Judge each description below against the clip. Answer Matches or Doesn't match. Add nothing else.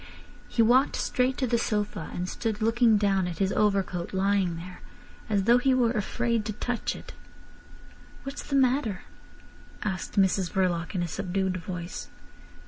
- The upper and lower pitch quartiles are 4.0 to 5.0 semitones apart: Matches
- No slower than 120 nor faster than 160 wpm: Matches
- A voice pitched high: Matches